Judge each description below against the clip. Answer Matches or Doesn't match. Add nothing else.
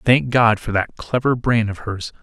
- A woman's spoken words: Doesn't match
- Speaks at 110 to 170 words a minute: Doesn't match